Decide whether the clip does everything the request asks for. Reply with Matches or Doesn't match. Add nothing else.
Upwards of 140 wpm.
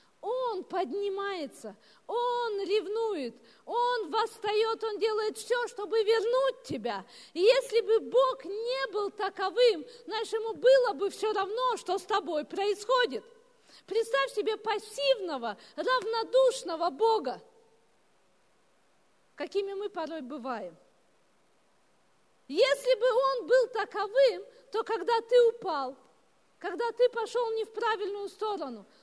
Doesn't match